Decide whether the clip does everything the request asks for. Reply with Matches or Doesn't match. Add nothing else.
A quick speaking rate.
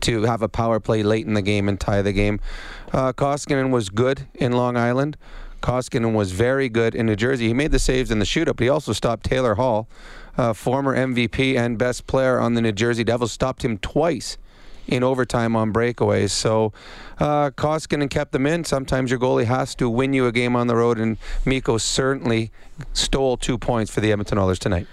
Matches